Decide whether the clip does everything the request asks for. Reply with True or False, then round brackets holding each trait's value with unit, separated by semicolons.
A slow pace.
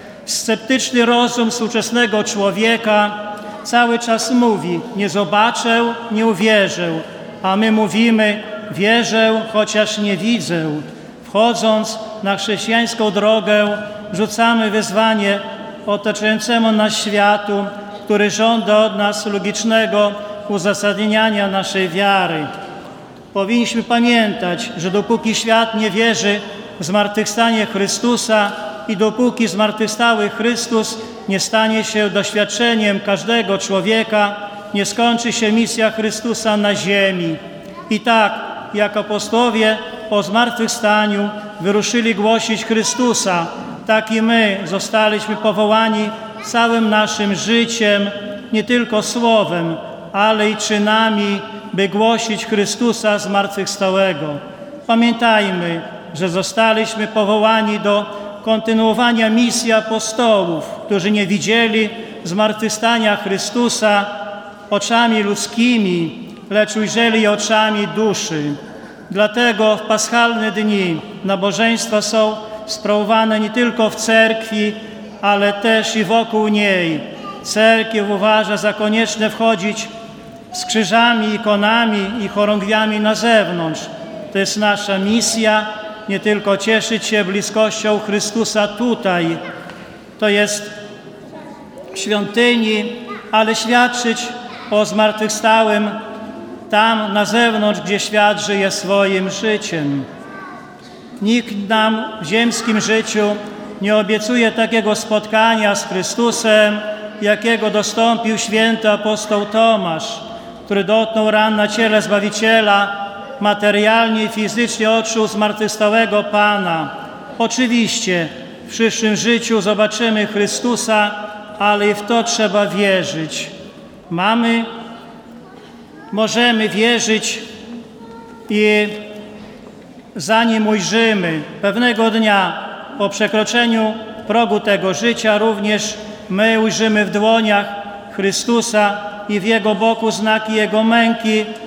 True (95 wpm)